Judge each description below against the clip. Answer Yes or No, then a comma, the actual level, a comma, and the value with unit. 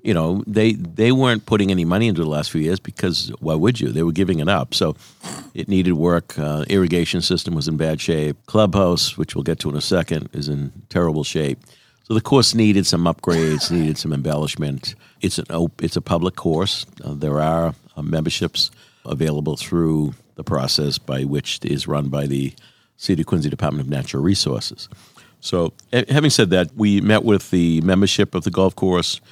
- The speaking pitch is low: Yes, very low, 85 Hz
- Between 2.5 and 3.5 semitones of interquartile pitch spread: No, average, 4.5 semitones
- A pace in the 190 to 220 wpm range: Yes, average, 200 wpm